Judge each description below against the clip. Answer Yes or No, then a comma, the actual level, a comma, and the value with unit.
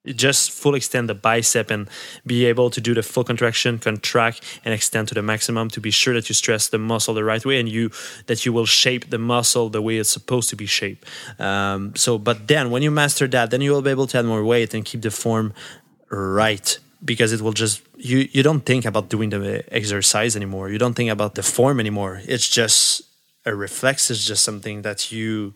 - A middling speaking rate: No, fast, 225 wpm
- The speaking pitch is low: Yes, low, 115 Hz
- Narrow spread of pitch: Yes, narrow, 2.2 semitones